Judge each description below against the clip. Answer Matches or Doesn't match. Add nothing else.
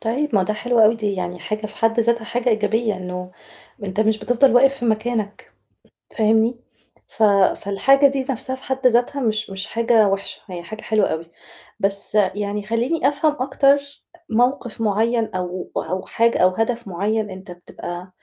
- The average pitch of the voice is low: Doesn't match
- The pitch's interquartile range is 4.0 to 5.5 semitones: Doesn't match